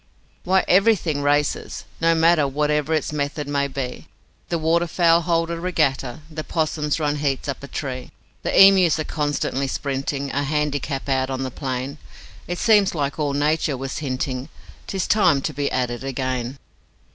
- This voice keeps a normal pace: Yes, average, 165 wpm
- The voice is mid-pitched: Yes, medium, 145 Hz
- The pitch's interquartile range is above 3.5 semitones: No, average, 3.0 semitones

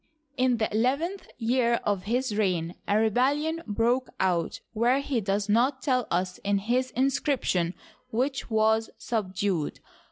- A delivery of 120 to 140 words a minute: Yes, slow, 135 wpm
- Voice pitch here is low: No, high, 230 Hz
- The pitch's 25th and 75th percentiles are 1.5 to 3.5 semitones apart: No, average, 4.2 semitones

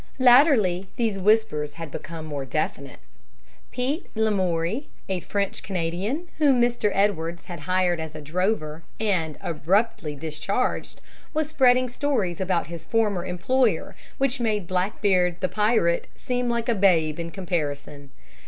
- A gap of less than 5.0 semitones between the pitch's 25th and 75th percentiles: No, wide, 5.6 semitones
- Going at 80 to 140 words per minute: Yes, slow, 135 wpm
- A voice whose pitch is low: No, high, 190 Hz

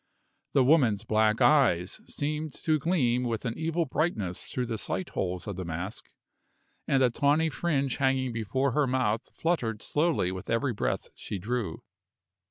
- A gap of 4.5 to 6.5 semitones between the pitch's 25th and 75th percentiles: Yes, wide, 5.6 semitones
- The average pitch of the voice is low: Yes, low, 125 Hz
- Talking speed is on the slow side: No, average, 160 wpm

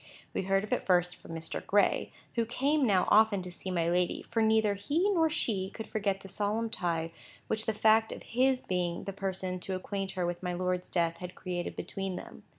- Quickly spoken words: Yes, fast, 215 wpm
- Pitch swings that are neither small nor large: Yes, average, 3.5 semitones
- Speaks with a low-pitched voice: No, high, 195 Hz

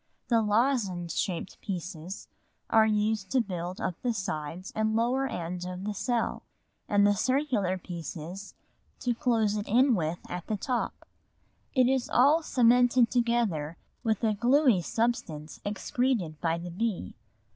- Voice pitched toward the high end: Yes, high, 210 Hz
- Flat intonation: No, average, 5.1 semitones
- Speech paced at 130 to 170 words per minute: Yes, average, 145 wpm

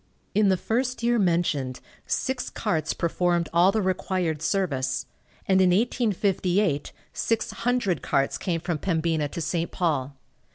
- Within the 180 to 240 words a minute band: No, slow, 135 wpm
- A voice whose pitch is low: No, medium, 180 Hz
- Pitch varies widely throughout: No, average, 4.1 semitones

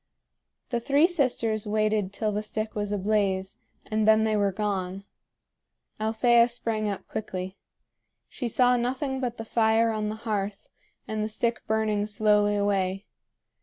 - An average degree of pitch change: No, narrow, 1.9 semitones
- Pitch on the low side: No, high, 215 Hz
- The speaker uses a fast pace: No, average, 145 wpm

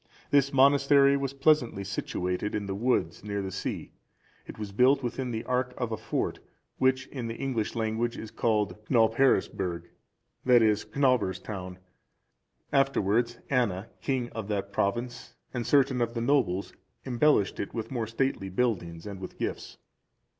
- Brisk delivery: No, average, 155 wpm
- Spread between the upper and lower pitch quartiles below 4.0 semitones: No, average, 4.4 semitones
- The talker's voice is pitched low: Yes, low, 115 Hz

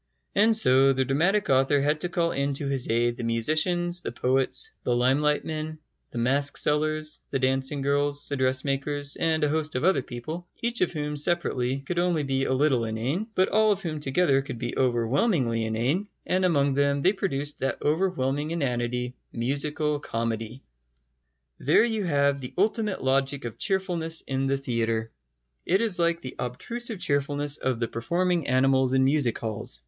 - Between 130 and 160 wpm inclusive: No, average, 175 wpm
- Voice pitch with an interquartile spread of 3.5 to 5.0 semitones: Yes, average, 4.5 semitones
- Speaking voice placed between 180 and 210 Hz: No, medium, 140 Hz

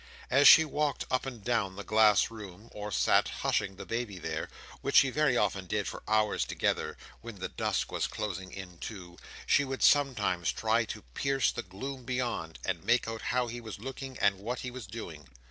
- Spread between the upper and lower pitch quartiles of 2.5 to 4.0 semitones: No, average, 4.7 semitones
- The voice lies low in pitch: Yes, low, 110 Hz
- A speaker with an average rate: Yes, average, 190 wpm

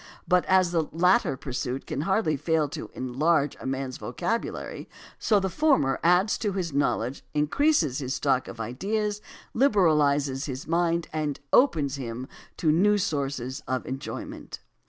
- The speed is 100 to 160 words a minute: Yes, average, 145 wpm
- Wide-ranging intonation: Yes, wide, 5.8 semitones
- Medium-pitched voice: Yes, medium, 150 Hz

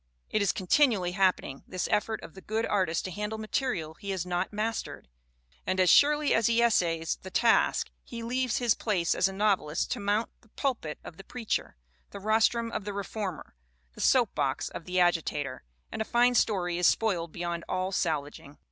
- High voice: Yes, high, 195 Hz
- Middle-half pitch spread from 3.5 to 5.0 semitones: Yes, average, 4.2 semitones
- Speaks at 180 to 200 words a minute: Yes, average, 185 wpm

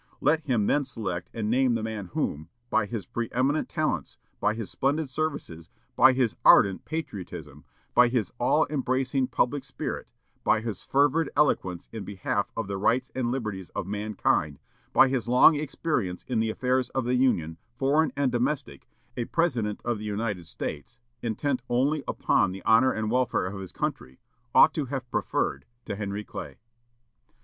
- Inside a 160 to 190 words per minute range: Yes, average, 165 wpm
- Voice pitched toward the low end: Yes, low, 120 Hz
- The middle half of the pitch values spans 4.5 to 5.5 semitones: Yes, average, 4.8 semitones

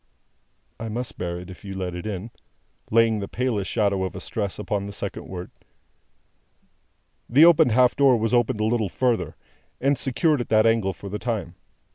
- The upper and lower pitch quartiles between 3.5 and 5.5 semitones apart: Yes, average, 3.8 semitones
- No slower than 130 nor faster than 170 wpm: No, average, 185 wpm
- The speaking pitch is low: Yes, low, 110 Hz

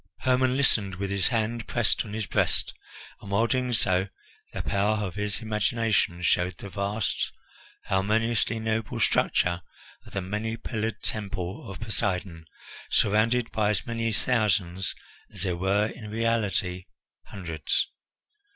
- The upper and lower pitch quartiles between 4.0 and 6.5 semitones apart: No, average, 2.9 semitones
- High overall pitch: No, low, 105 Hz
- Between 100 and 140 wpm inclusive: Yes, slow, 135 wpm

